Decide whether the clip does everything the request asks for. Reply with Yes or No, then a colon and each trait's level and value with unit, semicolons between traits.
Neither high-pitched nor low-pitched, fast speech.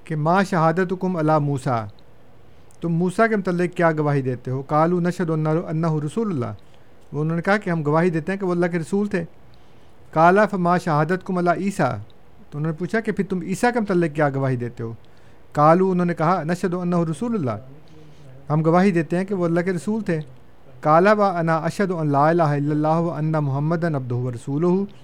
Yes: medium, 165 Hz; fast, 200 wpm